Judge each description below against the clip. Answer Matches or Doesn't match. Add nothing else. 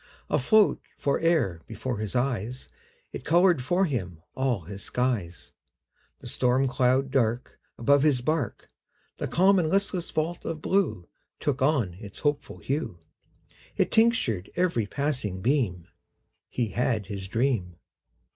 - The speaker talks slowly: Matches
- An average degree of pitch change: Doesn't match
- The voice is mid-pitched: Doesn't match